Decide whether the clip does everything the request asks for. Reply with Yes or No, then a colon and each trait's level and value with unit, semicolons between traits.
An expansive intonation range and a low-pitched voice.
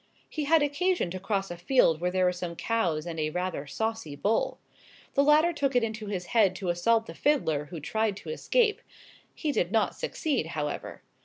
No: wide, 8.1 semitones; high, 205 Hz